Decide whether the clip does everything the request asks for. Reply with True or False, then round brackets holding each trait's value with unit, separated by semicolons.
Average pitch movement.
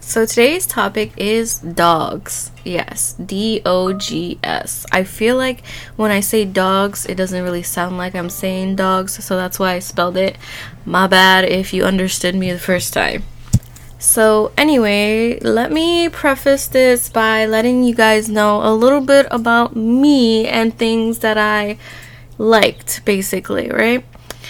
True (3.7 semitones)